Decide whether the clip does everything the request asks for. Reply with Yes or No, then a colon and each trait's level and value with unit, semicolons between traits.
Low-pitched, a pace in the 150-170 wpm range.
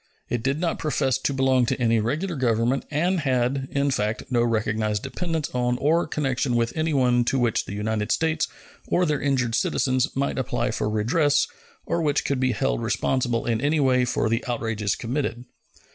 No: low, 130 Hz; average, 180 wpm